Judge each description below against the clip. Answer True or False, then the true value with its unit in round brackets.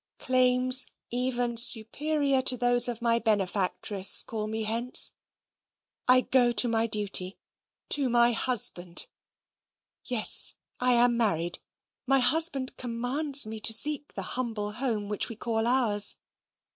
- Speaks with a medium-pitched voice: False (240 Hz)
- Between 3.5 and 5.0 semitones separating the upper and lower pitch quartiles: False (2.7 semitones)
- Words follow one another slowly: True (130 wpm)